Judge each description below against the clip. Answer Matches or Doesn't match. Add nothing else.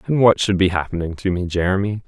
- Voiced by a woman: Doesn't match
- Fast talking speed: Matches